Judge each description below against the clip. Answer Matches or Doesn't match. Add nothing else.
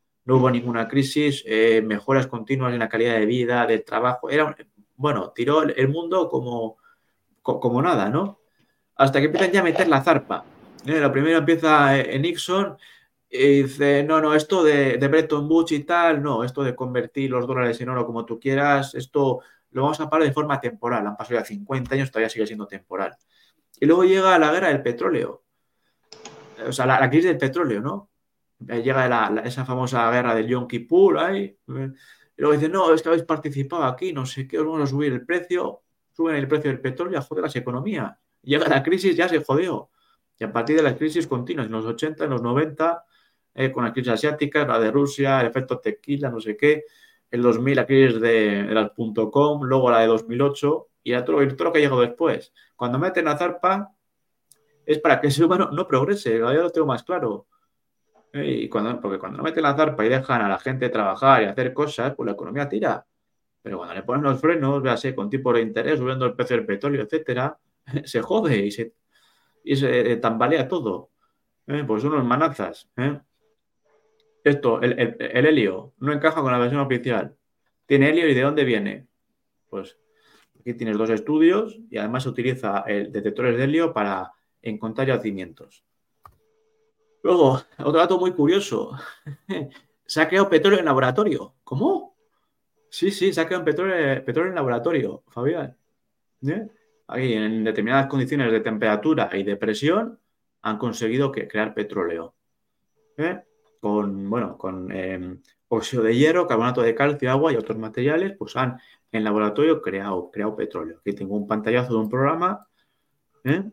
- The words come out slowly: Doesn't match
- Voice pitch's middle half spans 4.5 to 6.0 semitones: Matches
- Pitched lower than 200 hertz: Matches